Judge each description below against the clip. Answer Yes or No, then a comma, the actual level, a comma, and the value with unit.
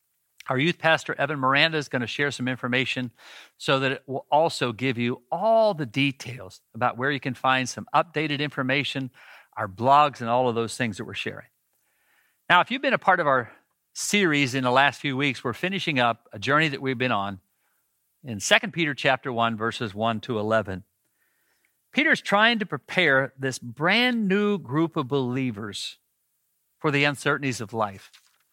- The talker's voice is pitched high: No, low, 135 Hz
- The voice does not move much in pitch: No, average, 4.0 semitones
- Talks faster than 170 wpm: Yes, average, 180 wpm